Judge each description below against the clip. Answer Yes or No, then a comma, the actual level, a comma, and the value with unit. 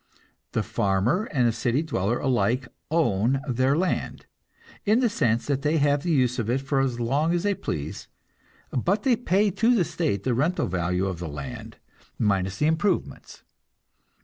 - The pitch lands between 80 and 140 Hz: Yes, low, 135 Hz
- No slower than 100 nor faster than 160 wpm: No, average, 175 wpm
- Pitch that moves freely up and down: Yes, wide, 6.8 semitones